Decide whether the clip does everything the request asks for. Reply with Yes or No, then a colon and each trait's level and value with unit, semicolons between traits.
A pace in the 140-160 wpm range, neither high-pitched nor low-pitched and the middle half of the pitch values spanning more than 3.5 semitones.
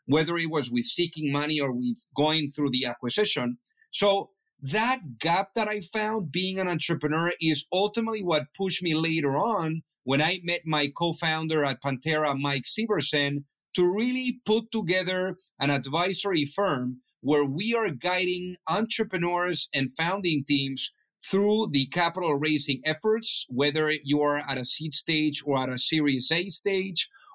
Yes: average, 155 wpm; medium, 160 Hz; average, 4.9 semitones